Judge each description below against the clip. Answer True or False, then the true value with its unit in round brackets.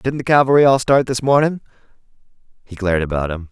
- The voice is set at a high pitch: False (120 Hz)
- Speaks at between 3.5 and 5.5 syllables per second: False (6.6 syllables/s)